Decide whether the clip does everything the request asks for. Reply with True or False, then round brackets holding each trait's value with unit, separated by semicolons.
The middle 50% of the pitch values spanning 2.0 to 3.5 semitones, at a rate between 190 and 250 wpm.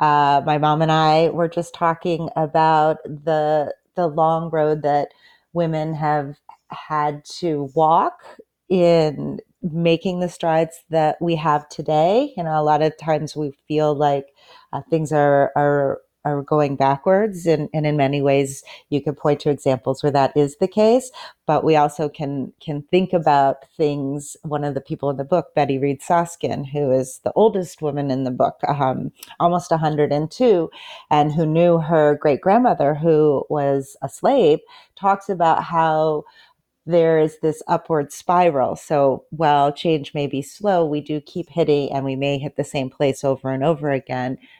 False (2.5 semitones; 170 wpm)